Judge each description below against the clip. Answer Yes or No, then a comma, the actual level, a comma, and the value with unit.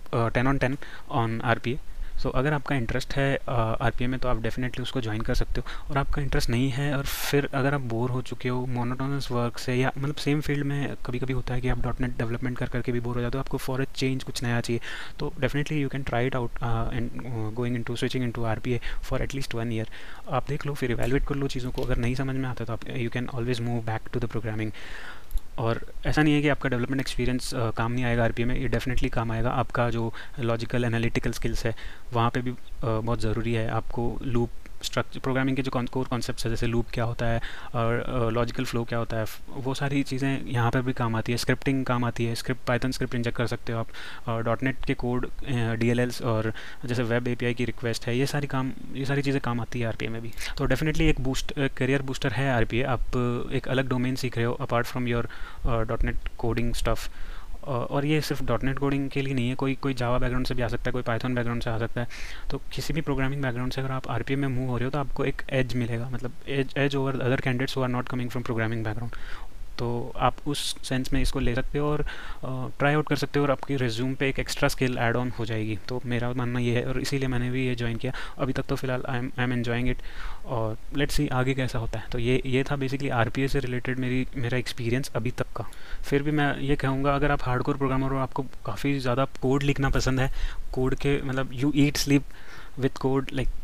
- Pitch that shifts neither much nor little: No, narrow, 2.3 semitones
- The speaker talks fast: Yes, fast, 250 wpm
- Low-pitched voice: Yes, low, 125 Hz